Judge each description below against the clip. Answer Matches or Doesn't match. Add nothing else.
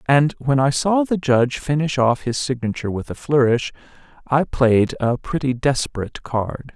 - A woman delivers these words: Doesn't match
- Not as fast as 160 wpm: Doesn't match